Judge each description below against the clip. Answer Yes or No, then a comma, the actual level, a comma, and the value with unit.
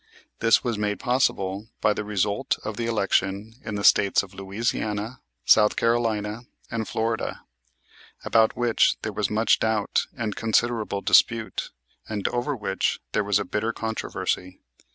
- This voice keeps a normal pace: Yes, average, 145 wpm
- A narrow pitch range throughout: Yes, narrow, 2.0 semitones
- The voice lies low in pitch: Yes, low, 110 Hz